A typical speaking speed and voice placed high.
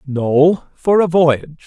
No: average, 145 wpm; medium, 155 Hz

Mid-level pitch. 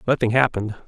No: low, 115 Hz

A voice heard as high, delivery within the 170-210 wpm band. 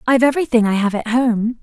No: high, 235 Hz; fast, 220 wpm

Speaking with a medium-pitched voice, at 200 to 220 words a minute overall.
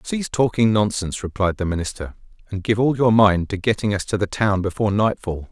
No: low, 105 Hz; fast, 205 wpm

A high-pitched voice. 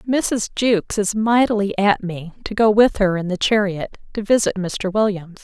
Yes: high, 205 Hz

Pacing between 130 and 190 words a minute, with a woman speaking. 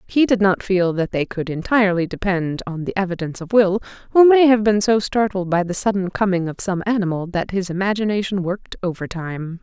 No: average, 200 wpm; female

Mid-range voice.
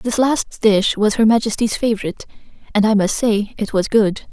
No: high, 215 Hz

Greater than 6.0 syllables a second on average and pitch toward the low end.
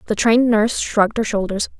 No: 6.5 syllables/s; high, 220 Hz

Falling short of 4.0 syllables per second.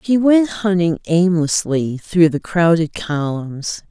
Yes: 3.5 syllables/s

